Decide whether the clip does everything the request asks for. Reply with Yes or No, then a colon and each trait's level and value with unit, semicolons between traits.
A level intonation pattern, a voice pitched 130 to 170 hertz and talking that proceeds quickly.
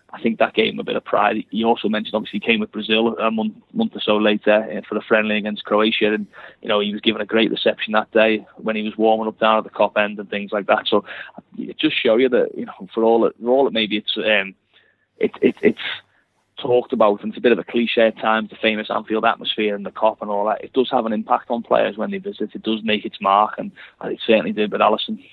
No: narrow, 1.3 semitones; low, 110 Hz; fast, 270 wpm